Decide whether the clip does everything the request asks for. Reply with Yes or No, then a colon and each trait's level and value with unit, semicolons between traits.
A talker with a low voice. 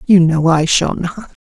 No: medium, 175 Hz